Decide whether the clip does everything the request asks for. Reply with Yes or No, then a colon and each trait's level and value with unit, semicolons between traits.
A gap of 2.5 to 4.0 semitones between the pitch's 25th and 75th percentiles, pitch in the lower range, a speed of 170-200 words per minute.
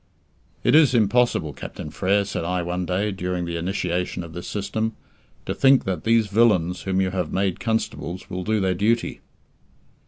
Yes: average, 3.4 semitones; very low, 95 Hz; average, 175 wpm